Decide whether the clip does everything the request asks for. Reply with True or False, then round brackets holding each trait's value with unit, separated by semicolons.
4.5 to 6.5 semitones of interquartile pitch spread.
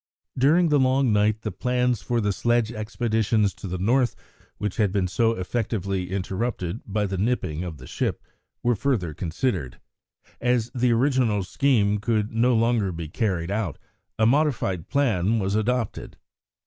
False (4.1 semitones)